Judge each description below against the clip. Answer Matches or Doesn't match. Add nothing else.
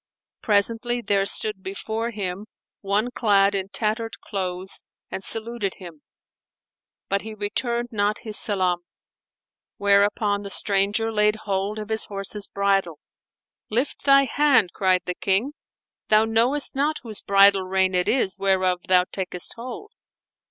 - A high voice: Matches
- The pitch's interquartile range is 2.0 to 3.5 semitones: Matches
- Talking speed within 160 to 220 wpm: Doesn't match